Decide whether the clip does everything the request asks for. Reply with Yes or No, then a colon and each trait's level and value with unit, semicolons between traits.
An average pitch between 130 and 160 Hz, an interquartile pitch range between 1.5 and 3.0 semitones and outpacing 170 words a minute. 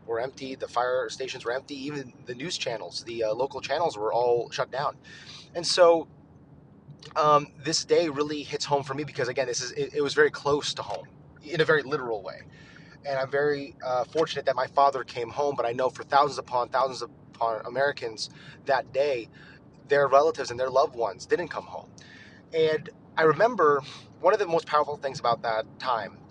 Yes: medium, 140 Hz; average, 2.7 semitones; average, 195 wpm